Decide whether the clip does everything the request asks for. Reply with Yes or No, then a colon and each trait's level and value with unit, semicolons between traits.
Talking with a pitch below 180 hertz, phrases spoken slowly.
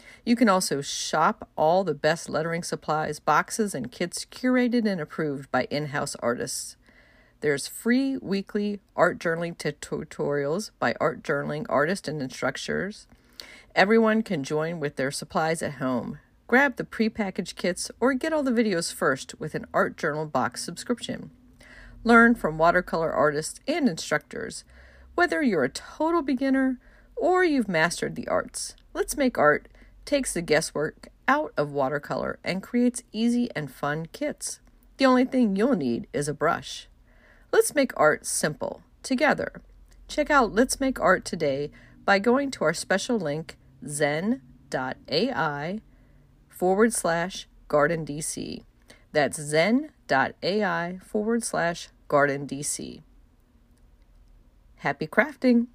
No: medium, 185 Hz; slow, 130 wpm